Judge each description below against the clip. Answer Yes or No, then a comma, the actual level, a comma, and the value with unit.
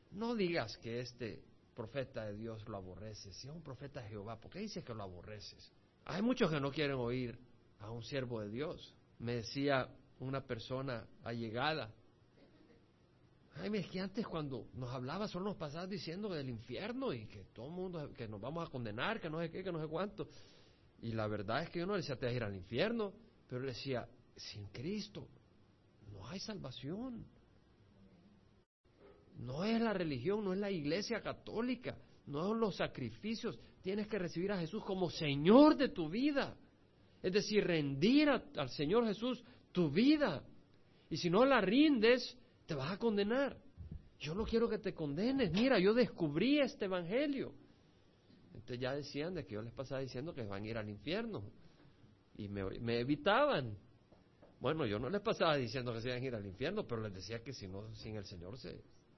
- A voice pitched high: No, medium, 145 Hz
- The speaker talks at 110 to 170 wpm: No, fast, 190 wpm